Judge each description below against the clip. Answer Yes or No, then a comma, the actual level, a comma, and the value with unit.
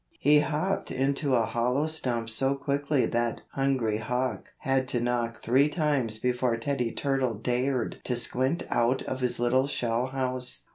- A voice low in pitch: Yes, low, 130 Hz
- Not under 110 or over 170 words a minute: Yes, average, 155 wpm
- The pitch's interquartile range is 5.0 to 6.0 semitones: No, narrow, 2.5 semitones